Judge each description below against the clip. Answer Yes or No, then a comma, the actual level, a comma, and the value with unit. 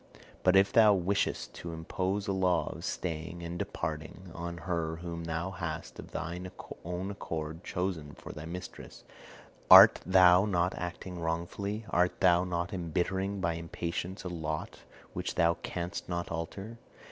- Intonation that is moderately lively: No, narrow, 2.0 semitones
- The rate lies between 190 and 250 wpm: No, average, 150 wpm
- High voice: No, very low, 85 Hz